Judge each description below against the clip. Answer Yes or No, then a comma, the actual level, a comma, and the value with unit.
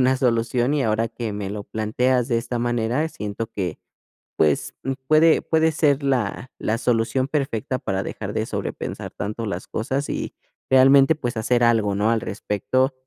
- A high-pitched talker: No, low, 120 Hz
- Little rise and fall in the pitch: No, average, 3.4 semitones